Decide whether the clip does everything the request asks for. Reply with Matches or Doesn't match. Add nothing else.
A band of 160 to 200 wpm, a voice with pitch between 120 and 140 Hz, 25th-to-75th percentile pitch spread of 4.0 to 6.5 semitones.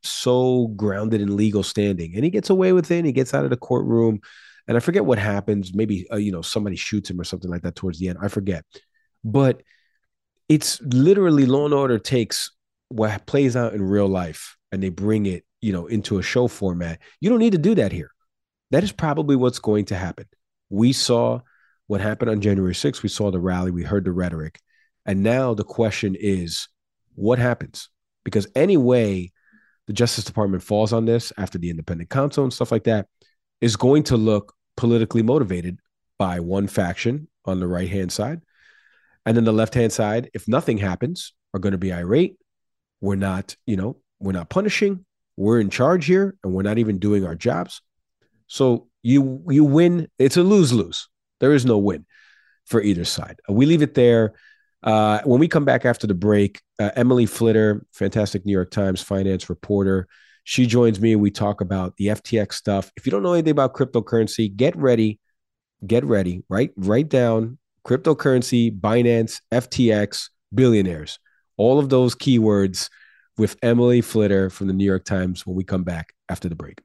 Doesn't match